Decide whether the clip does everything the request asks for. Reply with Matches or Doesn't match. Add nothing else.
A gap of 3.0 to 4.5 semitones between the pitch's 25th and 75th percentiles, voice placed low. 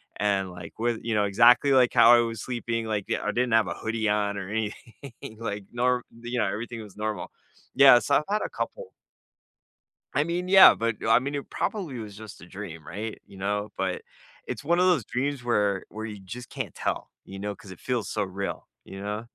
Matches